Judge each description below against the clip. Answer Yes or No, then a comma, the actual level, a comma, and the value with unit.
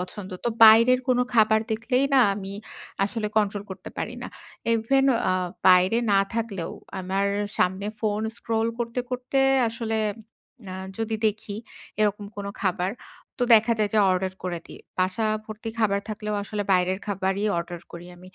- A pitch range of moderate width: Yes, average, 3.0 semitones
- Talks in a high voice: Yes, high, 210 Hz